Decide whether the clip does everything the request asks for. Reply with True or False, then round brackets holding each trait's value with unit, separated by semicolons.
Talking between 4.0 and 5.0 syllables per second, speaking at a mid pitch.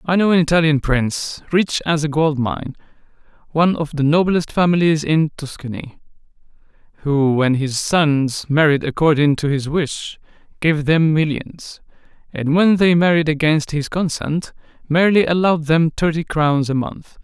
True (4.6 syllables/s; 155 Hz)